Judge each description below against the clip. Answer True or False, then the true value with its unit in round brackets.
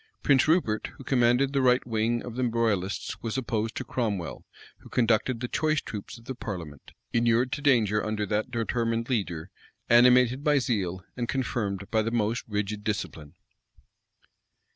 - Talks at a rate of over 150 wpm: True (160 wpm)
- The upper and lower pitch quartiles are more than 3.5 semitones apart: False (2.9 semitones)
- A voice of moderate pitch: False (115 Hz)